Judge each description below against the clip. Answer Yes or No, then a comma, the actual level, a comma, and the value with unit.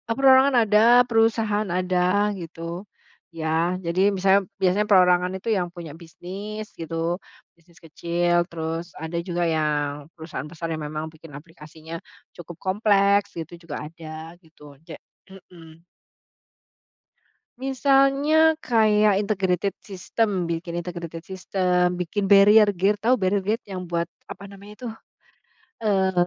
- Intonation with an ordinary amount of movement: Yes, average, 3.7 semitones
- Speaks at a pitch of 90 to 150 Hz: No, medium, 185 Hz